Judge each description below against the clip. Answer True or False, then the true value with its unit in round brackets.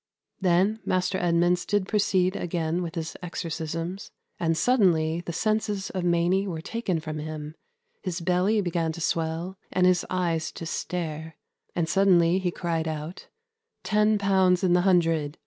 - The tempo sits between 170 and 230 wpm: False (155 wpm)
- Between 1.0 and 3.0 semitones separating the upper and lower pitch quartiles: True (2.5 semitones)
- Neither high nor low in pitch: True (175 Hz)